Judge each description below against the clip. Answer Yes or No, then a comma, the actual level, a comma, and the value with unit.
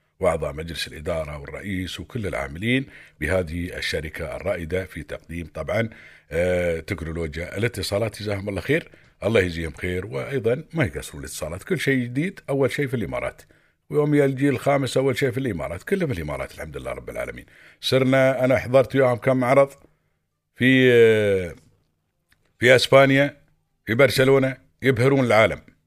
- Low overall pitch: Yes, low, 125 Hz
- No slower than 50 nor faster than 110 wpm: No, fast, 135 wpm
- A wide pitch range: Yes, wide, 6.6 semitones